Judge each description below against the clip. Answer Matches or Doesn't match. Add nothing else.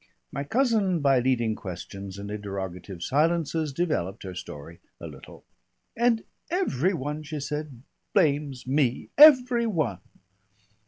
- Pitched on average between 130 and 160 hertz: Matches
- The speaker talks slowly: Matches